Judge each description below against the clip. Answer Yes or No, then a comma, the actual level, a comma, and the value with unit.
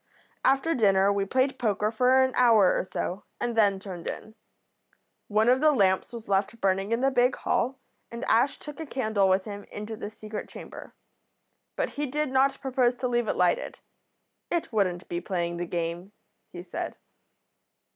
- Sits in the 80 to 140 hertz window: No, high, 220 Hz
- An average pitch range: Yes, average, 5.0 semitones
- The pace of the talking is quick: No, average, 175 wpm